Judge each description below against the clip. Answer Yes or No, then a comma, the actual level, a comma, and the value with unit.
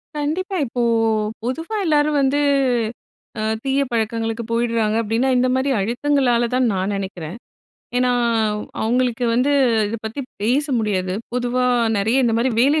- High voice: Yes, high, 245 Hz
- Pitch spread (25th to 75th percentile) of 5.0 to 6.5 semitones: No, average, 3.3 semitones